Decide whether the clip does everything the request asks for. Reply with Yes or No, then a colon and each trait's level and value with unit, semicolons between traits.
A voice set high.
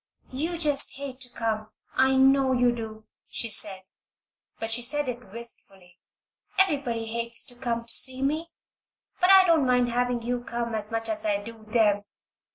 Yes: high, 240 Hz